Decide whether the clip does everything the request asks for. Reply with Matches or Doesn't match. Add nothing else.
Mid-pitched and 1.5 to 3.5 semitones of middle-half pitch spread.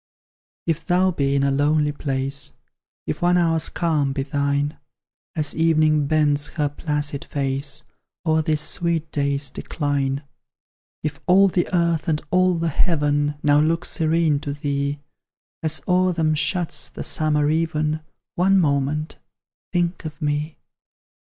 Matches